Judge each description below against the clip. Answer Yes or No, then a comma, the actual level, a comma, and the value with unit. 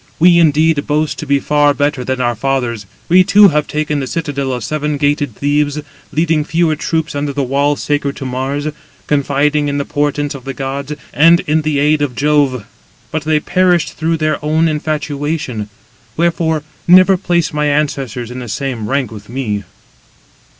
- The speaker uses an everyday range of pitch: No, narrow, 2.2 semitones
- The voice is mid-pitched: Yes, medium, 145 Hz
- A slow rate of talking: No, average, 175 wpm